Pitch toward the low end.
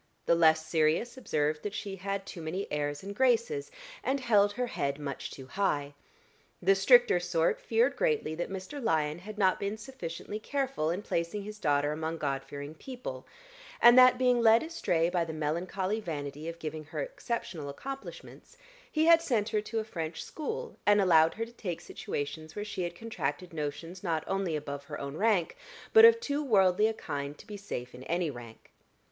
No: medium, 185 Hz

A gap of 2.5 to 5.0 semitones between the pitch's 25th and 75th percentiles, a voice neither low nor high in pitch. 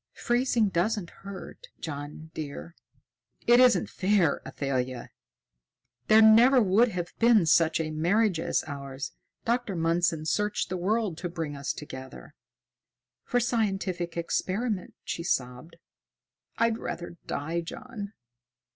No: wide, 5.6 semitones; medium, 180 Hz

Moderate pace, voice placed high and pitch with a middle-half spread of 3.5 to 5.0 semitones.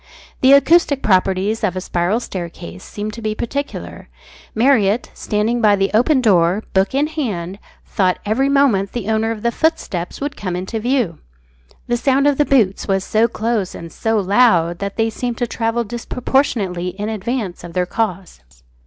Yes: average, 170 wpm; high, 215 Hz; average, 4.4 semitones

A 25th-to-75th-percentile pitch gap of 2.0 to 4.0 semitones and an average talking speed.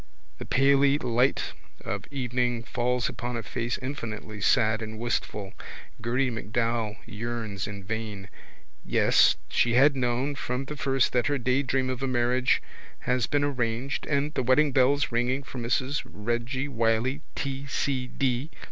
Yes: average, 2.7 semitones; average, 150 wpm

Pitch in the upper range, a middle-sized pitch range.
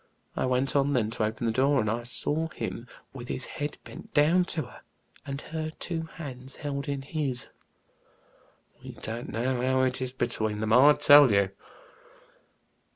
No: low, 130 Hz; average, 3.3 semitones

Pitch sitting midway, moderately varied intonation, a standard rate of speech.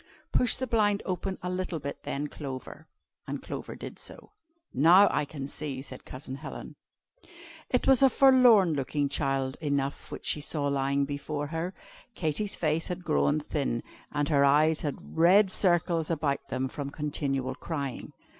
Yes: medium, 150 Hz; average, 4.4 semitones; average, 160 wpm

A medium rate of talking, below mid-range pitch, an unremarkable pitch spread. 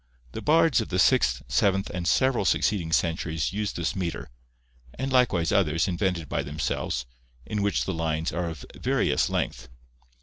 Yes: average, 160 wpm; very low, 85 Hz; average, 4.1 semitones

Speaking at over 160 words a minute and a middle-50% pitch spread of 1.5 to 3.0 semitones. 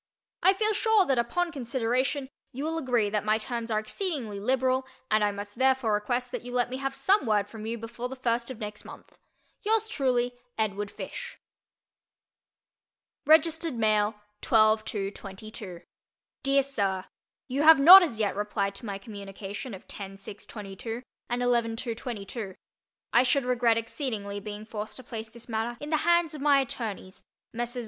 No: average, 170 wpm; average, 4.1 semitones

